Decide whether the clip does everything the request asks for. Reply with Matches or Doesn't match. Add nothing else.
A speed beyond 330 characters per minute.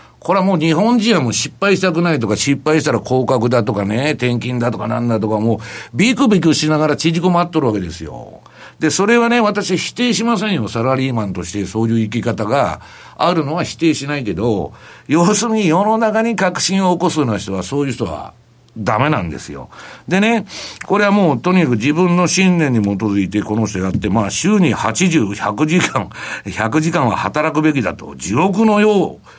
Matches